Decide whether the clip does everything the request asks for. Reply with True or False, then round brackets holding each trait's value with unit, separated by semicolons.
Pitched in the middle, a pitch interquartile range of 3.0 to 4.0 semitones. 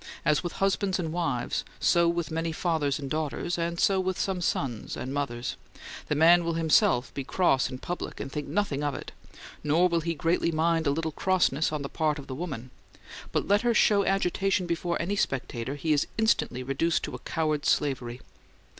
True (160 Hz; 3.7 semitones)